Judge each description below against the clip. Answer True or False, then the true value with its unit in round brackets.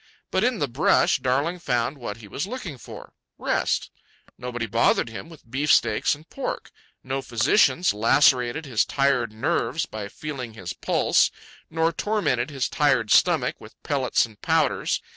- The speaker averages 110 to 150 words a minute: True (145 wpm)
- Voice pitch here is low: True (130 Hz)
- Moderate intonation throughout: True (4.9 semitones)